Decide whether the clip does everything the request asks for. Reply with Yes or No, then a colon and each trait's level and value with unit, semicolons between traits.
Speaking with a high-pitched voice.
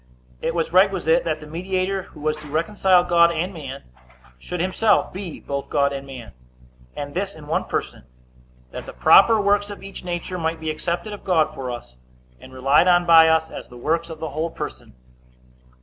No: medium, 165 Hz